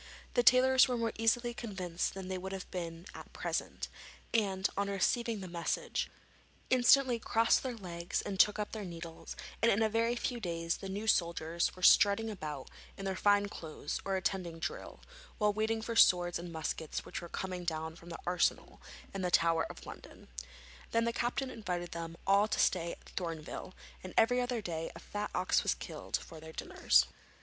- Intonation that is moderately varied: Yes, average, 4.7 semitones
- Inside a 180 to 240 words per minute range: Yes, average, 190 wpm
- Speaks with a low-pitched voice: No, high, 190 Hz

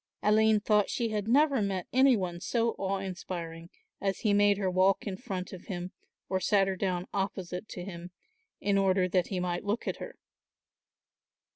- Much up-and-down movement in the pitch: No, narrow, 2.4 semitones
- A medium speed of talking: Yes, average, 180 wpm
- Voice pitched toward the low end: No, high, 195 Hz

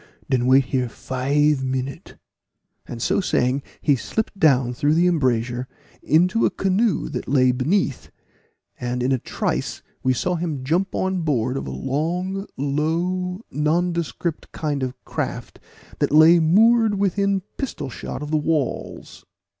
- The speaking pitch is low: No, medium, 150 Hz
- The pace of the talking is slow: No, average, 145 wpm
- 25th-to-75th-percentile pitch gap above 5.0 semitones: Yes, wide, 5.6 semitones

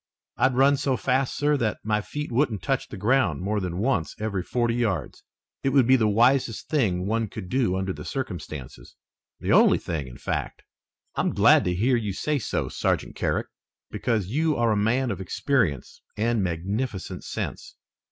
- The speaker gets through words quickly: No, average, 180 wpm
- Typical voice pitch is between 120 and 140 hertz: No, low, 110 Hz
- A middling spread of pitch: No, wide, 5.7 semitones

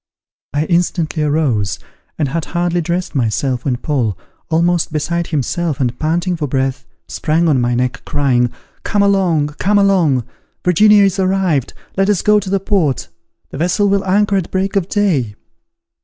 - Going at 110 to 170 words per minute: Yes, average, 160 wpm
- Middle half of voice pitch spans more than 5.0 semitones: Yes, wide, 5.6 semitones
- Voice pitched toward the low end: No, medium, 165 Hz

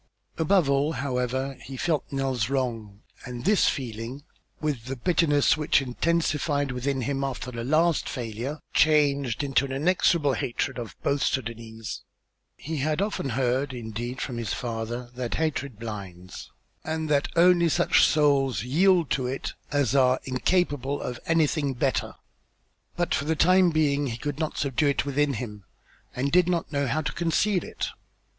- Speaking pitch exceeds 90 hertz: Yes, medium, 140 Hz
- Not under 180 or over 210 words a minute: No, average, 155 wpm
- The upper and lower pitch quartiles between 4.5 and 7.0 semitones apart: No, average, 3.7 semitones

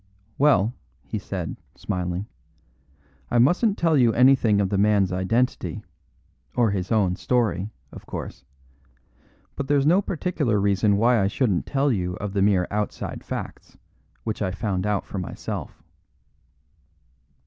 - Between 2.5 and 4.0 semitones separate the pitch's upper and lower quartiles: No, average, 4.7 semitones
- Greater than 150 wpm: No, slow, 135 wpm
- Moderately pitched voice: No, low, 105 Hz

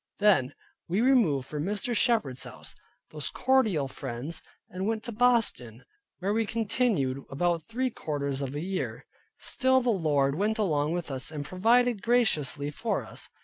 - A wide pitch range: Yes, wide, 7.9 semitones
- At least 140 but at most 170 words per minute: Yes, average, 150 wpm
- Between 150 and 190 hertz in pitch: Yes, medium, 185 Hz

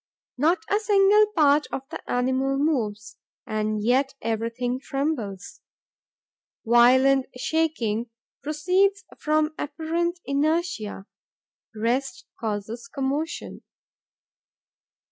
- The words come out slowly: Yes, slow, 85 wpm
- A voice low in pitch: No, very high, 275 Hz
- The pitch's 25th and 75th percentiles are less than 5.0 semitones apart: No, average, 5.3 semitones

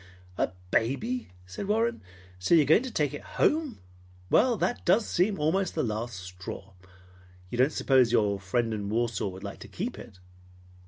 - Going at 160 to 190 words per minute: Yes, average, 175 wpm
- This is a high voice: No, low, 130 Hz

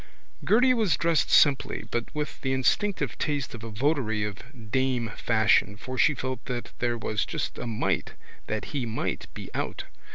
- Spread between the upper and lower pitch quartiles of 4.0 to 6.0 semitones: Yes, average, 4.4 semitones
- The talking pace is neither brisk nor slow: Yes, average, 170 wpm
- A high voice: No, low, 125 Hz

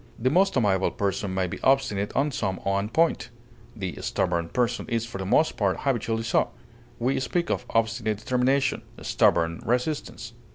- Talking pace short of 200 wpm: Yes, average, 160 wpm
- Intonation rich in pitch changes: No, average, 4.8 semitones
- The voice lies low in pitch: Yes, low, 115 Hz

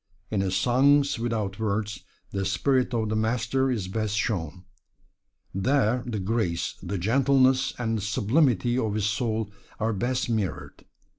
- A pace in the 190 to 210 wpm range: No, average, 145 wpm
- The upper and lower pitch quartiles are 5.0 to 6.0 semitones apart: No, average, 3.8 semitones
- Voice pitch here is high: No, low, 110 Hz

